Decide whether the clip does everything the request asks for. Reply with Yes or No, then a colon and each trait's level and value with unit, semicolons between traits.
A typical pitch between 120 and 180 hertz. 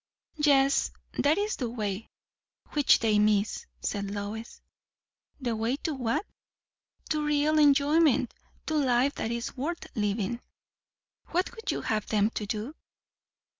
No: high, 245 Hz